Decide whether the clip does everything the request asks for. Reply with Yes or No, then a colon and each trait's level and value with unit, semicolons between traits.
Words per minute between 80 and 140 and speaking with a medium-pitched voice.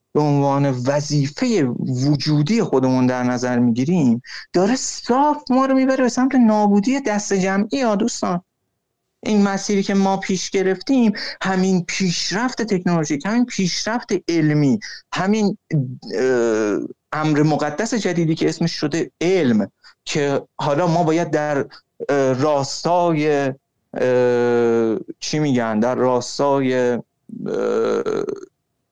Yes: slow, 105 wpm; medium, 170 Hz